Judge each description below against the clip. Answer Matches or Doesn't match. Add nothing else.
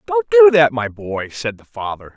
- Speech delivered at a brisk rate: Matches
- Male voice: Matches